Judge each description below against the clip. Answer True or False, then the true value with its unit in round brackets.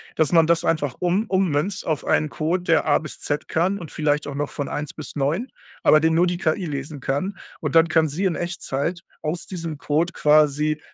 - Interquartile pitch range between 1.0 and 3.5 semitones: True (2.8 semitones)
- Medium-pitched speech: True (160 Hz)